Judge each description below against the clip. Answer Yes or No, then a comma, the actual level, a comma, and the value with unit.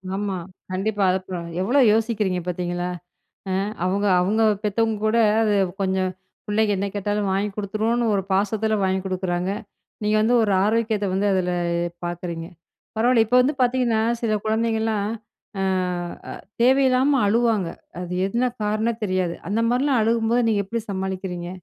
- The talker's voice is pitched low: No, high, 210 Hz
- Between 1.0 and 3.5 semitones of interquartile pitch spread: Yes, average, 3.2 semitones